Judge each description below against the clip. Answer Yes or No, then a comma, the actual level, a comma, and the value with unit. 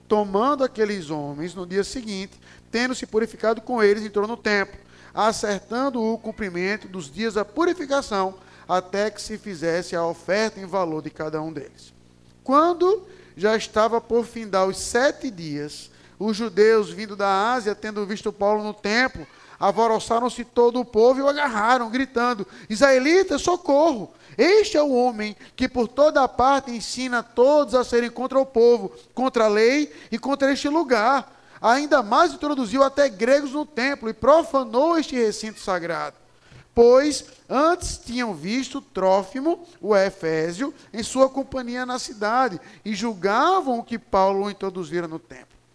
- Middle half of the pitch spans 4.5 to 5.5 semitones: Yes, average, 5.0 semitones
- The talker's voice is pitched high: Yes, high, 230 Hz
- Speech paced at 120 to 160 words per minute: Yes, average, 150 wpm